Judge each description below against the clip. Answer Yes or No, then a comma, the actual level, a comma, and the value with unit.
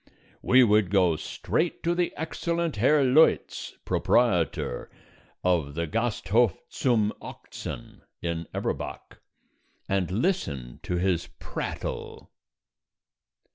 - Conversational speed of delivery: No, slow, 95 wpm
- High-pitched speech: No, low, 105 Hz